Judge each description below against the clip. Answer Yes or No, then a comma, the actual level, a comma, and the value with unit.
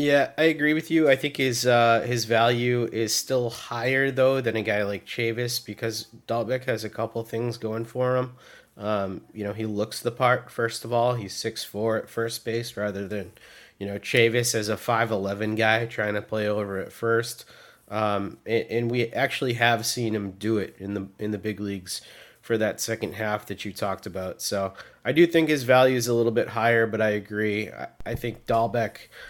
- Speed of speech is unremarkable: No, fast, 210 wpm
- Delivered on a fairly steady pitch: Yes, narrow, 2.3 semitones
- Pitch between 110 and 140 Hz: Yes, low, 115 Hz